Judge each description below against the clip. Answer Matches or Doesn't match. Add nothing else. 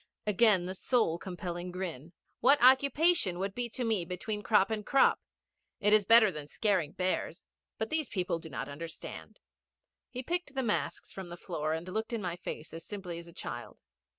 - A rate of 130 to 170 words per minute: Doesn't match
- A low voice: Doesn't match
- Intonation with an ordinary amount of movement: Matches